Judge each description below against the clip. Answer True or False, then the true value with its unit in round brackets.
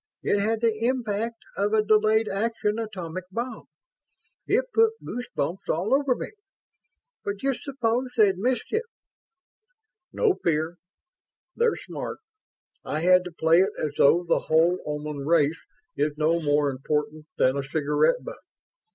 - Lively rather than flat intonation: True (6.6 semitones)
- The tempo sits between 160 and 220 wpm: False (145 wpm)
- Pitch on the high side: True (195 Hz)